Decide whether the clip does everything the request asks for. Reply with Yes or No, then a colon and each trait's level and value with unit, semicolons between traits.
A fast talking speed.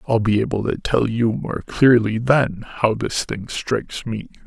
No: average, 190 wpm